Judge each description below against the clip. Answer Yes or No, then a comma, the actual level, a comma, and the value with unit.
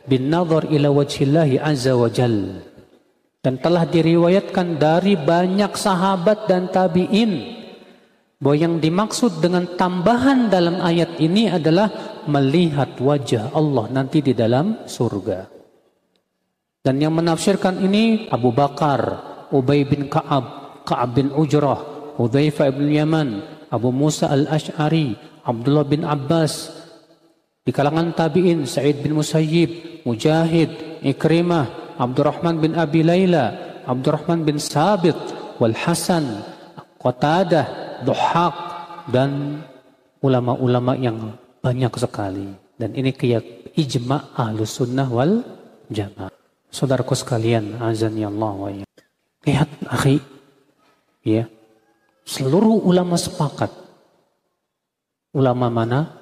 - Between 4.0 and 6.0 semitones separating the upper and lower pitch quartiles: Yes, average, 4.5 semitones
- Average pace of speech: Yes, average, 105 wpm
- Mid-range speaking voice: Yes, medium, 150 Hz